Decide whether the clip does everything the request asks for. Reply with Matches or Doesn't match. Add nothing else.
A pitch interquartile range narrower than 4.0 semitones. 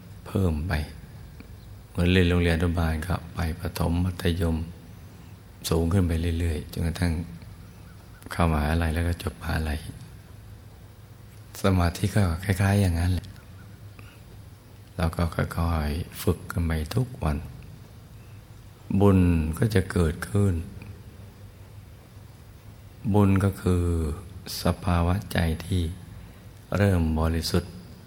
Matches